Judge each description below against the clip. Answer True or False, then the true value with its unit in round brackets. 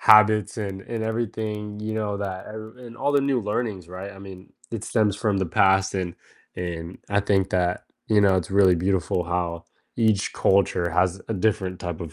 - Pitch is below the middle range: True (100 Hz)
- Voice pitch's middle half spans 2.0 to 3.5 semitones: True (2.9 semitones)